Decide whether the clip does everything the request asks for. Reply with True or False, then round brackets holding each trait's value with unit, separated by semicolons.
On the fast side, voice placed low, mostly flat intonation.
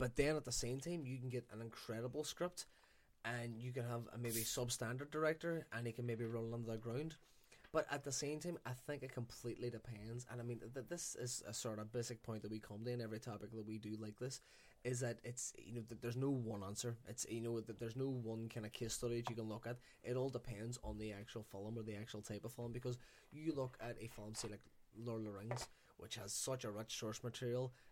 True (255 wpm; 120 Hz; 2.1 semitones)